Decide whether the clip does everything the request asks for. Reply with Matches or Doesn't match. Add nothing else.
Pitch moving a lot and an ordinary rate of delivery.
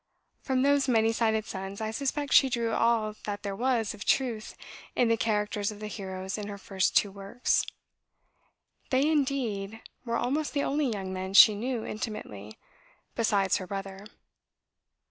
Doesn't match